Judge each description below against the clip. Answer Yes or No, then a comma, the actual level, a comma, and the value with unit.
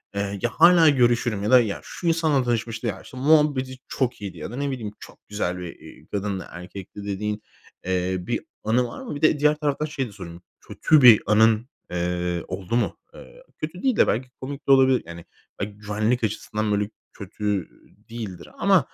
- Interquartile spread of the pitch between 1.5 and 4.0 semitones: No, average, 5.2 semitones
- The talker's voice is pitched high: No, low, 110 Hz